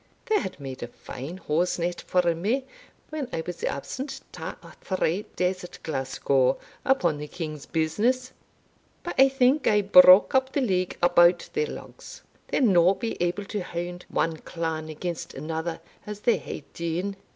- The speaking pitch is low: No, medium, 180 Hz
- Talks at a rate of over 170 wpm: No, average, 165 wpm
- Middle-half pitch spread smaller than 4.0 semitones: No, average, 4.5 semitones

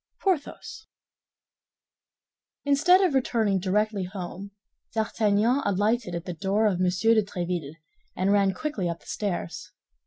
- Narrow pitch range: No, average, 3.9 semitones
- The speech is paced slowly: Yes, slow, 125 wpm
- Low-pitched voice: No, high, 200 Hz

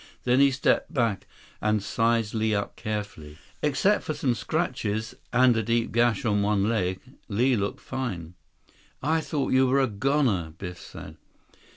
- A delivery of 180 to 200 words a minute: No, average, 160 wpm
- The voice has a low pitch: Yes, low, 115 Hz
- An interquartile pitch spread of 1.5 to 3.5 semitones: No, average, 4.3 semitones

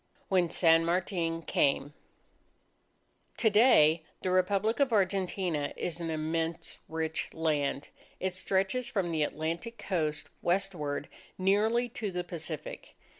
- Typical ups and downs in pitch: Yes, average, 3.5 semitones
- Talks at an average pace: No, slow, 120 wpm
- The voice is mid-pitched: Yes, medium, 175 Hz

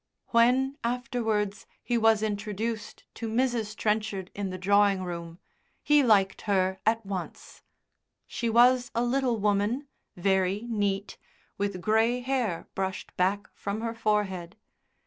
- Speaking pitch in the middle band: No, high, 215 Hz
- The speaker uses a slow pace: Yes, slow, 125 wpm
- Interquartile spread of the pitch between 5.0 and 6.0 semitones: No, average, 3.2 semitones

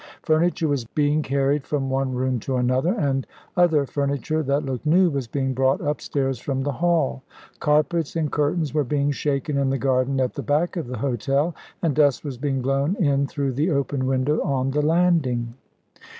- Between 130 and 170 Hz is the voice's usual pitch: Yes, medium, 140 Hz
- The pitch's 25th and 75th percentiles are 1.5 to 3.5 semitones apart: Yes, narrow, 2.4 semitones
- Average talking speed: Yes, average, 185 wpm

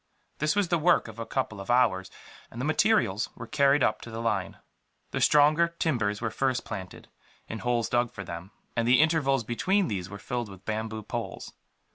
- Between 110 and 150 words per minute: No, average, 195 wpm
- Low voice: Yes, low, 120 Hz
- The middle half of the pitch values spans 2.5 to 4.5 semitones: No, average, 5.3 semitones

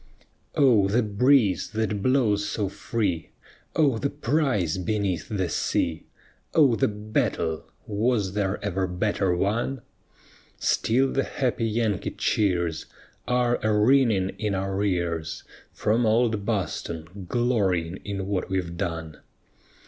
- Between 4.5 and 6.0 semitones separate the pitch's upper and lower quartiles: No, average, 3.9 semitones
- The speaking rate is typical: No, slow, 120 wpm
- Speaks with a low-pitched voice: Yes, low, 105 Hz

